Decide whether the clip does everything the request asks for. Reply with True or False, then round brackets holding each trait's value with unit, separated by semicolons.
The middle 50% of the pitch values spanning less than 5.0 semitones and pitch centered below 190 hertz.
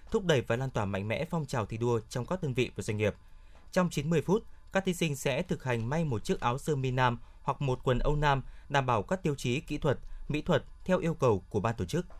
False (5.5 semitones; 135 Hz)